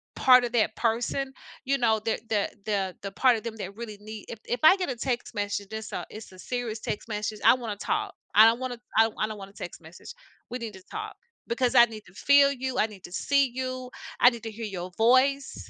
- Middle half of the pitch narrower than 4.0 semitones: Yes, average, 3.3 semitones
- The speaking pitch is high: Yes, high, 230 Hz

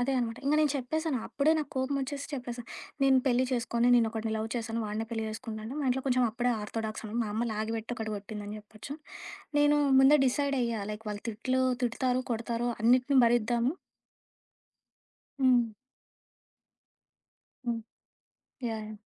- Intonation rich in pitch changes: No, average, 2.8 semitones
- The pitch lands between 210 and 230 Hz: No, high, 240 Hz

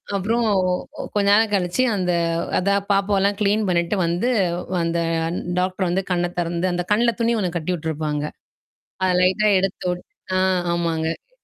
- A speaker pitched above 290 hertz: No, medium, 185 Hz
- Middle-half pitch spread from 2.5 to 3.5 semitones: Yes, average, 2.8 semitones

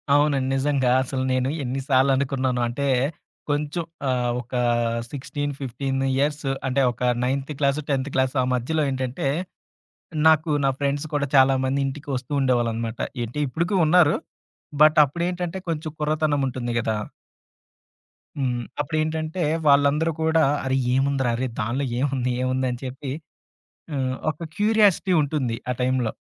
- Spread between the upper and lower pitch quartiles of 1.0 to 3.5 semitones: Yes, average, 2.8 semitones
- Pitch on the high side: No, low, 135 Hz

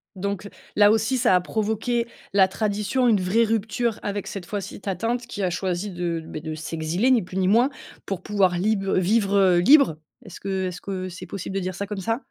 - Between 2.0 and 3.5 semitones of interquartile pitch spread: Yes, average, 3.2 semitones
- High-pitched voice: Yes, high, 200 Hz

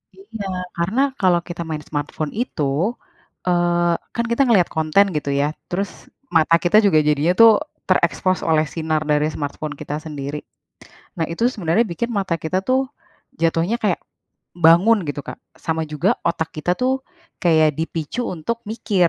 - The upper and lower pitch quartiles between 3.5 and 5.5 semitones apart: Yes, average, 4.0 semitones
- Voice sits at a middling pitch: Yes, medium, 170 Hz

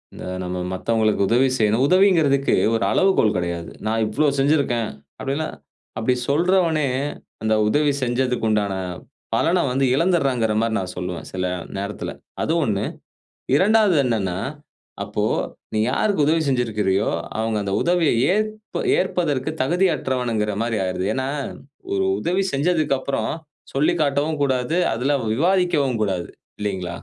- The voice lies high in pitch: No, low, 130 Hz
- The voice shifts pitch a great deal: Yes, wide, 6.7 semitones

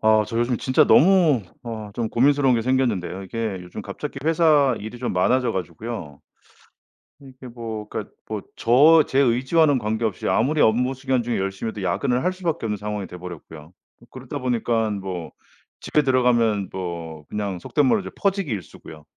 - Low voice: Yes, low, 115 Hz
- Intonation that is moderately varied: Yes, average, 4.8 semitones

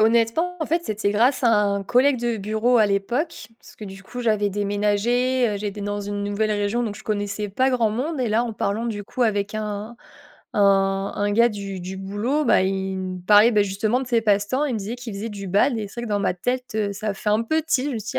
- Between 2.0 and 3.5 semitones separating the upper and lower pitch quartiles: Yes, average, 2.9 semitones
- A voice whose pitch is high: Yes, high, 210 Hz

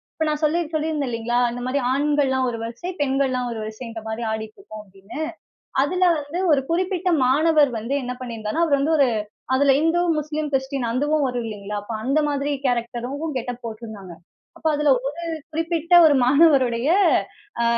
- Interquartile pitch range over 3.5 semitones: Yes, average, 4.3 semitones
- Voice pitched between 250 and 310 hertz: Yes, very high, 270 Hz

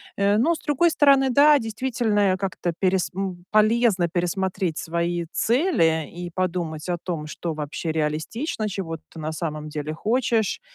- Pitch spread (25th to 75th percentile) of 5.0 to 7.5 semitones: Yes, wide, 5.5 semitones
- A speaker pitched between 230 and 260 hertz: No, medium, 185 Hz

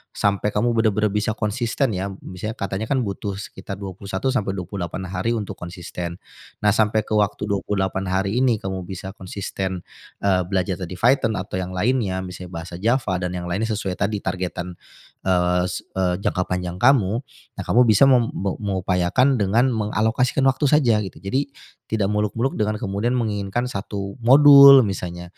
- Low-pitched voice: Yes, low, 100 Hz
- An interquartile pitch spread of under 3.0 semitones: No, average, 3.4 semitones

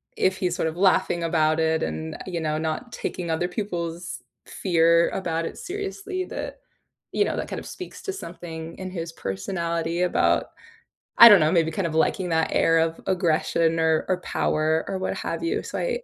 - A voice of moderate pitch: Yes, medium, 170 Hz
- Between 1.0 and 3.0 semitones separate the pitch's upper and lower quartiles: Yes, narrow, 2.5 semitones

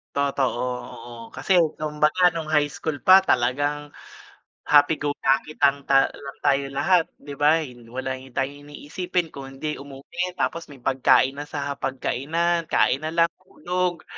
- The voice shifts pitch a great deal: No, average, 3.0 semitones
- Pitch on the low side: No, medium, 145 Hz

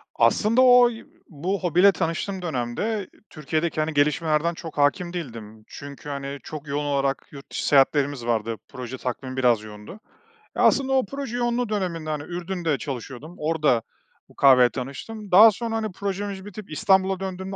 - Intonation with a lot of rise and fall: Yes, wide, 6.3 semitones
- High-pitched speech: No, medium, 165 Hz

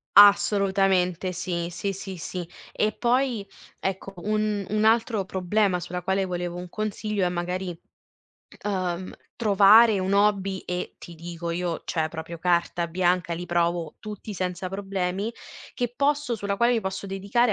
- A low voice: No, high, 190 Hz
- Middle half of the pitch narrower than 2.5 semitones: No, average, 2.8 semitones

